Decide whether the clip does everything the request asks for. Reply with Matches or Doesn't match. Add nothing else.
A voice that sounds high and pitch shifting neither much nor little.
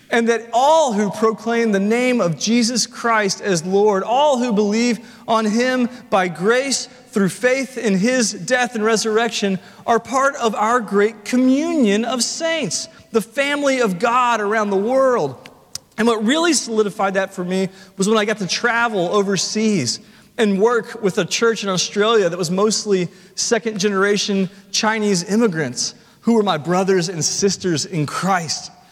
Matches